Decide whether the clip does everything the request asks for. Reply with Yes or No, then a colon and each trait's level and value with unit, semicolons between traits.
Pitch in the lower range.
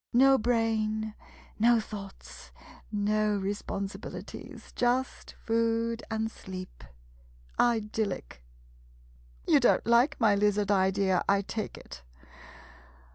No: high, 215 Hz